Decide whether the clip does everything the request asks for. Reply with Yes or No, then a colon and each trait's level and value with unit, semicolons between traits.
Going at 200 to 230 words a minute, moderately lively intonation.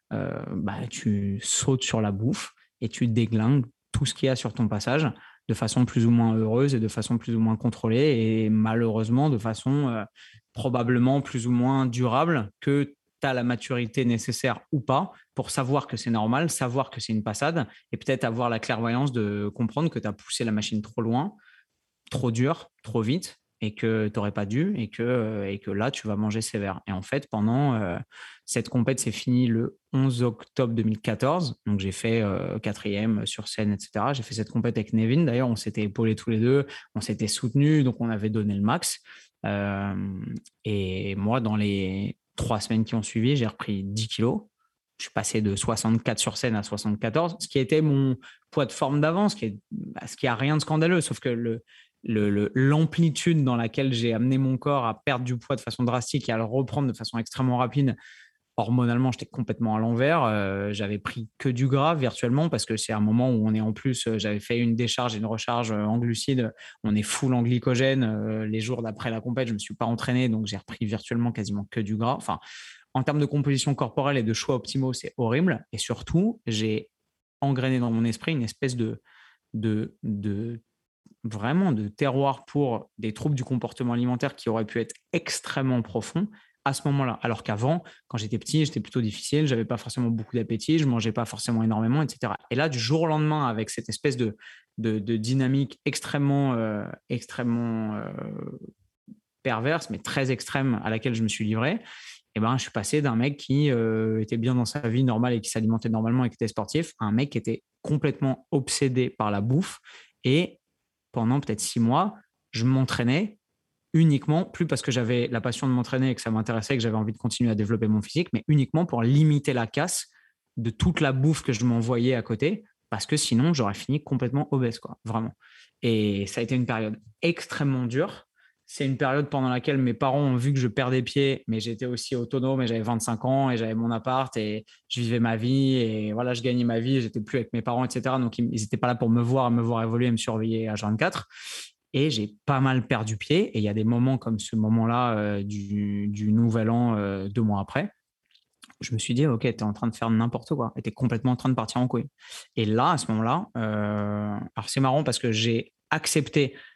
Yes: average, 215 wpm; average, 3.2 semitones